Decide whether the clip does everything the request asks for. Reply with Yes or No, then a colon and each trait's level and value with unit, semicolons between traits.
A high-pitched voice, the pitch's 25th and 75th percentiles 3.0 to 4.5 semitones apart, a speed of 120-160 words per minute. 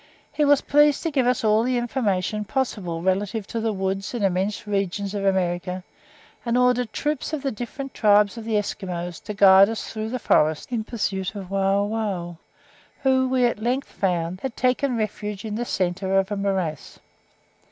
No: high, 210 Hz; average, 4.1 semitones; average, 180 wpm